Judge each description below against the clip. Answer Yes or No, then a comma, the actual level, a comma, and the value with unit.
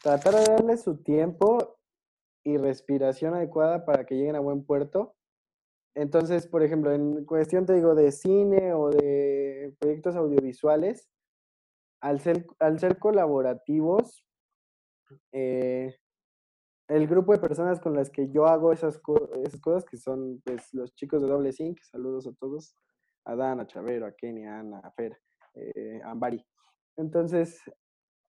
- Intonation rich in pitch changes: No, average, 4.4 semitones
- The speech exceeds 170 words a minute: No, average, 150 wpm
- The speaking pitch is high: No, medium, 150 Hz